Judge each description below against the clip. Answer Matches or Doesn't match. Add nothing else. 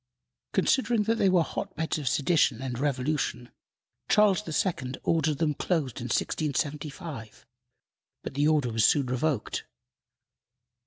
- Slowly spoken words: Matches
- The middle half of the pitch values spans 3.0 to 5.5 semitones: Matches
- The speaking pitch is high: Doesn't match